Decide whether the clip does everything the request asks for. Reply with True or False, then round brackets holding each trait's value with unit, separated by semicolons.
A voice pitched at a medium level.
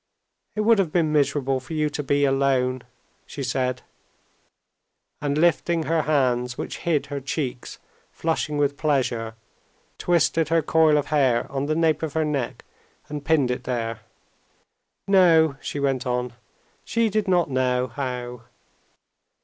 True (145 Hz)